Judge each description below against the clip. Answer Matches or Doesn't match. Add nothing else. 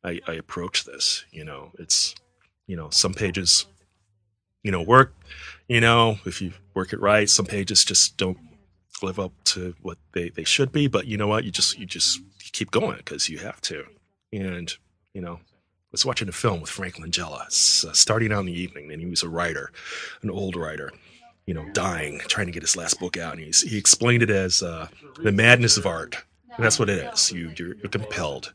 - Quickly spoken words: Matches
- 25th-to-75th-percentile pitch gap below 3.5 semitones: Matches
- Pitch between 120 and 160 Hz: Doesn't match